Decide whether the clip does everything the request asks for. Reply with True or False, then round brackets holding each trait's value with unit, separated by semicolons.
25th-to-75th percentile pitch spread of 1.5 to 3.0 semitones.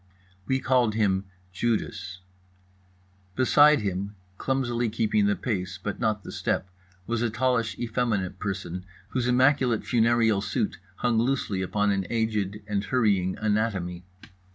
False (3.4 semitones)